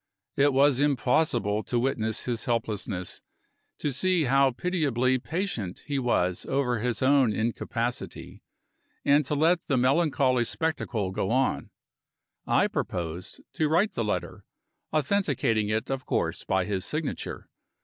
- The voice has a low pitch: Yes, low, 130 Hz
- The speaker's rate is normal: No, slow, 130 wpm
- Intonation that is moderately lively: Yes, average, 4.8 semitones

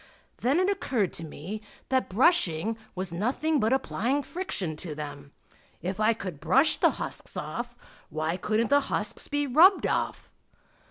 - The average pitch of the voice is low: No, high, 215 Hz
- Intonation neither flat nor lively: No, wide, 8.4 semitones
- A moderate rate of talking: Yes, average, 155 wpm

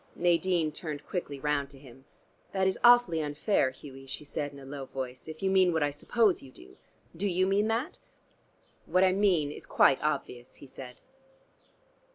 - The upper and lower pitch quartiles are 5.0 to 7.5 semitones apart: Yes, wide, 5.4 semitones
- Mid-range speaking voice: Yes, medium, 155 Hz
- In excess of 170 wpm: Yes, average, 185 wpm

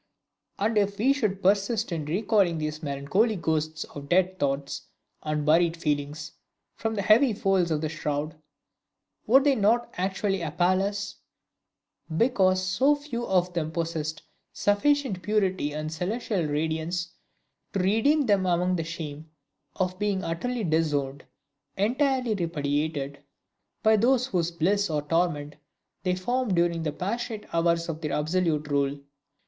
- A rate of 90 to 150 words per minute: Yes, average, 140 wpm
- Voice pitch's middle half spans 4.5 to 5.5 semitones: Yes, average, 5.0 semitones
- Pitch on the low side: No, medium, 180 Hz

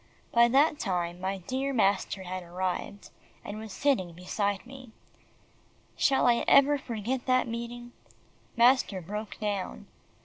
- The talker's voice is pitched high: Yes, high, 220 Hz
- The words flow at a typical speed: No, slow, 130 wpm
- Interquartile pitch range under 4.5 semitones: No, average, 5.2 semitones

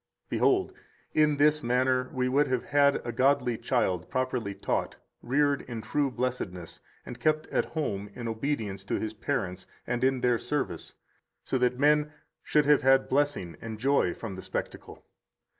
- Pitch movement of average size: Yes, average, 4.2 semitones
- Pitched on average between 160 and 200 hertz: No, low, 130 Hz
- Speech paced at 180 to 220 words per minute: No, average, 165 wpm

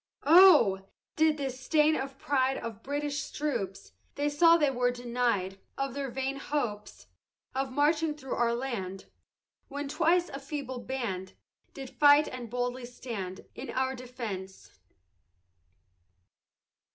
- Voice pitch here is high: Yes, very high, 265 Hz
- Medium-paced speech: No, slow, 125 wpm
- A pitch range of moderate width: Yes, average, 3.4 semitones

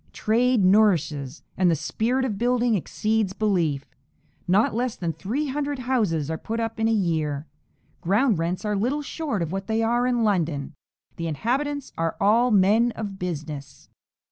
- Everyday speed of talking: Yes, average, 165 wpm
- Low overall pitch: No, high, 210 Hz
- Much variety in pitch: Yes, wide, 6.1 semitones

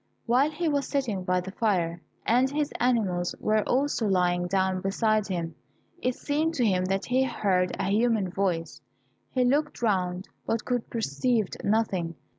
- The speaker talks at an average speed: Yes, average, 160 wpm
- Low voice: No, high, 210 Hz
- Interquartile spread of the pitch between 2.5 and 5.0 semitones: No, wide, 5.4 semitones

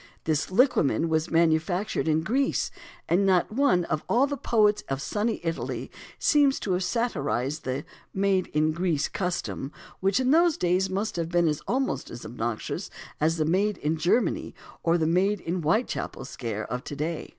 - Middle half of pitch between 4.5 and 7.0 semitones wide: Yes, average, 5.0 semitones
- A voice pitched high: No, medium, 175 Hz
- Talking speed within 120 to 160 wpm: No, average, 170 wpm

